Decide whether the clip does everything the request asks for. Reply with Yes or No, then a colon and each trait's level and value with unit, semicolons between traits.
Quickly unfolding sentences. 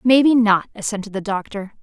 No: average, 165 wpm